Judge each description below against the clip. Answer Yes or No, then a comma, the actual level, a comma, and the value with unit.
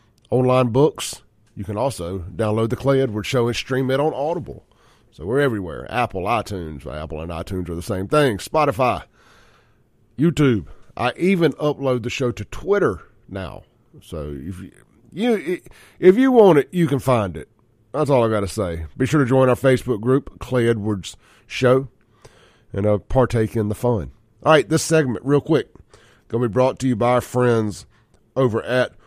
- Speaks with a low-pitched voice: Yes, low, 120 Hz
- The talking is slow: No, average, 180 wpm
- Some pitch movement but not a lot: Yes, average, 4.2 semitones